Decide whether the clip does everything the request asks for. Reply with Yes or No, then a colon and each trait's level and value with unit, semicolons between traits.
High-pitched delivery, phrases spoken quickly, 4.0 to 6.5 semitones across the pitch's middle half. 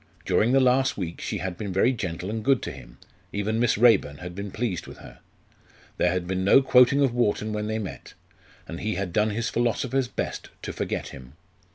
No: low, 105 Hz; fast, 210 wpm; average, 4.8 semitones